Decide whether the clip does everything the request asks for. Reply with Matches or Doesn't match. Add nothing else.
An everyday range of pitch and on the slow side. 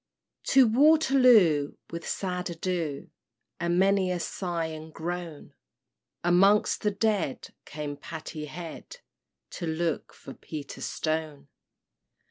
Matches